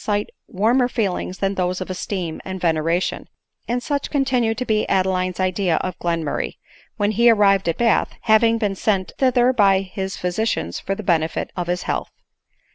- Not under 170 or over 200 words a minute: Yes, average, 175 wpm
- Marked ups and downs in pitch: No, average, 3.6 semitones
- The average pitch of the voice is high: Yes, high, 195 Hz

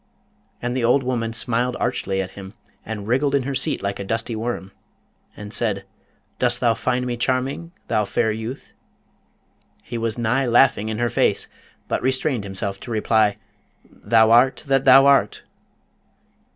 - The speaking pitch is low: Yes, low, 120 Hz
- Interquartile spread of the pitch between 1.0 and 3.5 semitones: Yes, average, 2.8 semitones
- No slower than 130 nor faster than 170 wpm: Yes, average, 160 wpm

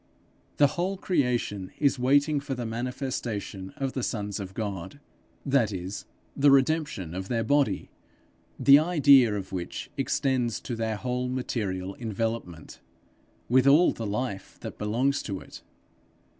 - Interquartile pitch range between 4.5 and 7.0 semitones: Yes, average, 5.1 semitones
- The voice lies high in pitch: No, low, 120 Hz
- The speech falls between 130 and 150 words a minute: Yes, average, 140 wpm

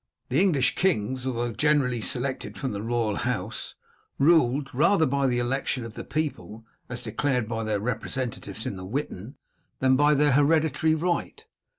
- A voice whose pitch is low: Yes, low, 130 Hz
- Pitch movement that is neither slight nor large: Yes, average, 4.2 semitones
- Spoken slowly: No, average, 160 wpm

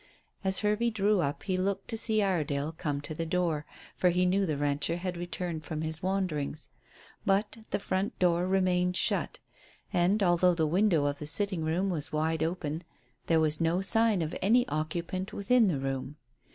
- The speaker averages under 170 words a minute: No, average, 180 wpm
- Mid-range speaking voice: Yes, medium, 175 Hz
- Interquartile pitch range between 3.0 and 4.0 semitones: Yes, average, 3.6 semitones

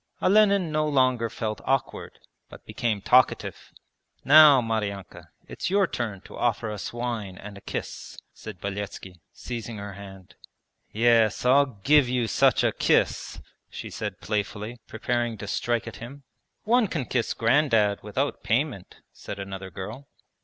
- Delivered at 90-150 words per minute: Yes, average, 145 wpm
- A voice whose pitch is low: Yes, low, 115 Hz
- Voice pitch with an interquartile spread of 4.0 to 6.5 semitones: Yes, average, 4.4 semitones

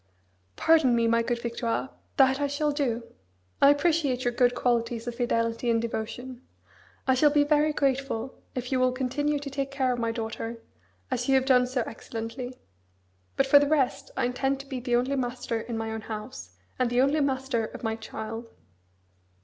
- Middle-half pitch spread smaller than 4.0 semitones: Yes, average, 2.9 semitones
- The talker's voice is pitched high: Yes, very high, 250 Hz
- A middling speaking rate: Yes, average, 190 wpm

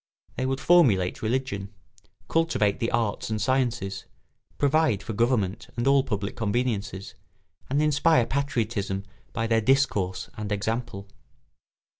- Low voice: Yes, low, 115 Hz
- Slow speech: Yes, slow, 120 wpm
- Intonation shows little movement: No, average, 4.6 semitones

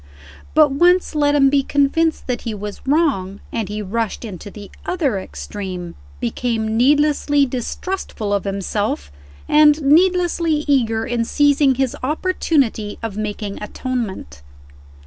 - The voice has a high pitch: Yes, very high, 250 Hz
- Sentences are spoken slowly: Yes, slow, 125 wpm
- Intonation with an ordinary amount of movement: No, wide, 6.1 semitones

